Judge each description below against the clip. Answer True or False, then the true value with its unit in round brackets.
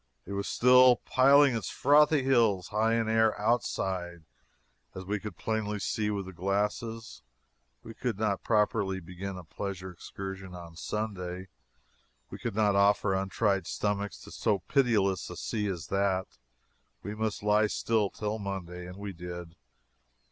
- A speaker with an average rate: True (150 wpm)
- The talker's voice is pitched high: False (100 Hz)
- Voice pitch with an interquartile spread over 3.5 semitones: False (2.7 semitones)